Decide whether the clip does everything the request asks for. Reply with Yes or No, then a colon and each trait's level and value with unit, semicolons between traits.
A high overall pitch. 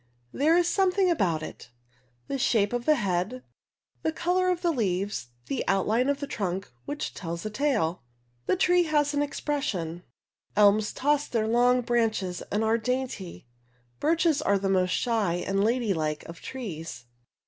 Yes: high, 225 Hz